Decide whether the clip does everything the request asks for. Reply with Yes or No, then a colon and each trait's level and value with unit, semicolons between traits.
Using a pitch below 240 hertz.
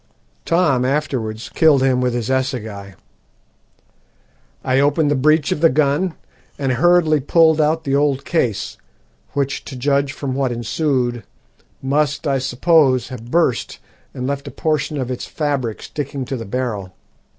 Yes: medium, 140 Hz